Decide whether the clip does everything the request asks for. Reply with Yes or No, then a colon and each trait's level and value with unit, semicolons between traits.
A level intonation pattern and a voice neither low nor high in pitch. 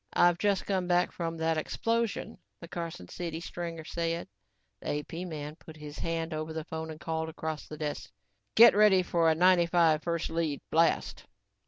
Yes: narrow, 1.8 semitones; medium, 165 Hz